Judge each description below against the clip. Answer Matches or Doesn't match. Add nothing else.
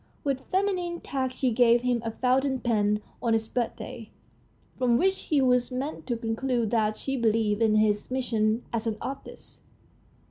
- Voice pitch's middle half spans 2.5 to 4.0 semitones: Matches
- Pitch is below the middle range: Doesn't match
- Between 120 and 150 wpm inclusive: Doesn't match